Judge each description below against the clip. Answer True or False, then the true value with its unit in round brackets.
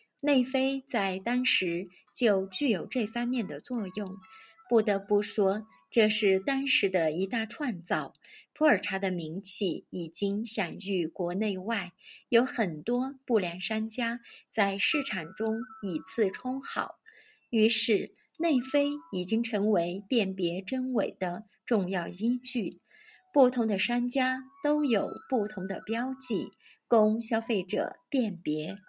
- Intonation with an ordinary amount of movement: True (4.6 semitones)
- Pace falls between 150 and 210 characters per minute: True (185 characters per minute)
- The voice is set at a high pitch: True (220 Hz)